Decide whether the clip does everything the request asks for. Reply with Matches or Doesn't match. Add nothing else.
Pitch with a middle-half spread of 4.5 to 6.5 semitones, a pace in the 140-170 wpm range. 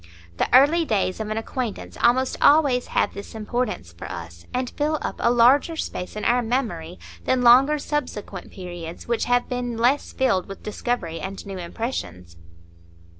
Matches